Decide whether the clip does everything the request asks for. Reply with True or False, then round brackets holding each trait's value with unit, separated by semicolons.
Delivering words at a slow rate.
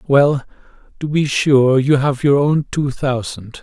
False (165 wpm)